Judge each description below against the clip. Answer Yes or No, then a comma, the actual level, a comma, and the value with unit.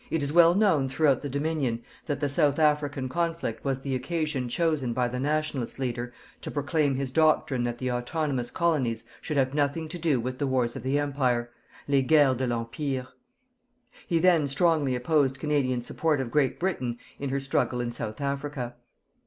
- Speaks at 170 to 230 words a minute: Yes, average, 180 wpm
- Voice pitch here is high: No, medium, 140 Hz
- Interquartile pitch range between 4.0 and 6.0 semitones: No, average, 3.3 semitones